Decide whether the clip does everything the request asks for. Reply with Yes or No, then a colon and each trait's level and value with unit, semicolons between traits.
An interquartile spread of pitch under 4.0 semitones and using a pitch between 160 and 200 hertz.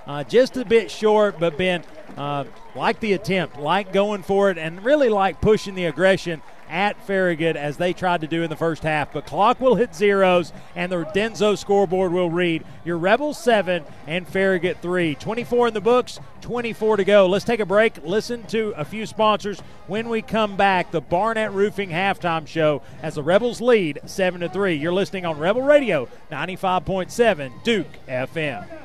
No: average, 4.3 semitones; high, 190 Hz